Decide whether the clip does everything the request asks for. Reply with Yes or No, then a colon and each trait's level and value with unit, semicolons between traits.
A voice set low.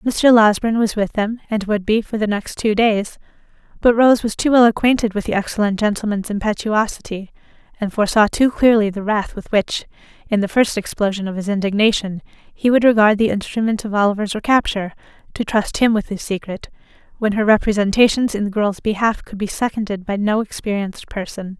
No: high, 210 Hz